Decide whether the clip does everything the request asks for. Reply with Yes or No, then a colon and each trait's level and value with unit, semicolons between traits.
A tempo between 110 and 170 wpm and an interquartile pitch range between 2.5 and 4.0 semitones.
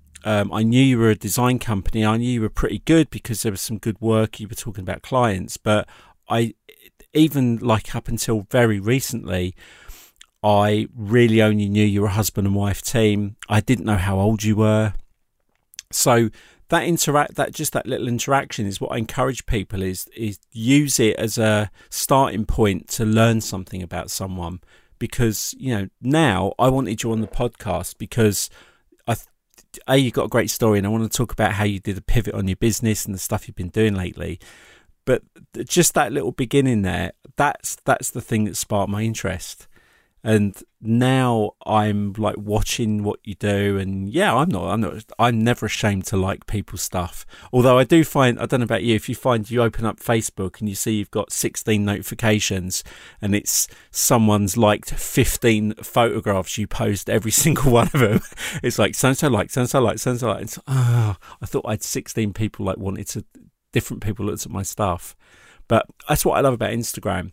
No: average, 200 wpm; average, 2.8 semitones